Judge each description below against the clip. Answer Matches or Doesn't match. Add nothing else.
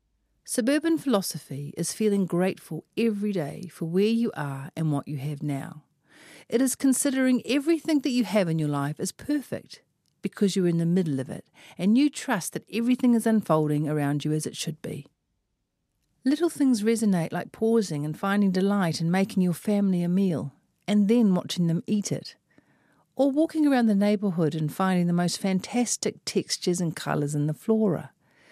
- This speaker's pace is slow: Doesn't match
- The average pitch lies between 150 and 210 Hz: Matches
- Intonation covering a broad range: Matches